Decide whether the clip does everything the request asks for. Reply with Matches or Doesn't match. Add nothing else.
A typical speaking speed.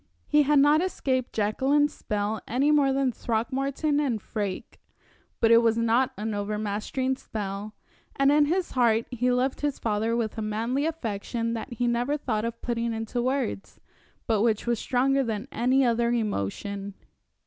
Matches